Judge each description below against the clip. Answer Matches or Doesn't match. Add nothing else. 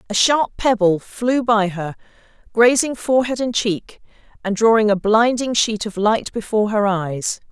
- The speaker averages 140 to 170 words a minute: Matches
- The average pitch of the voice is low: Doesn't match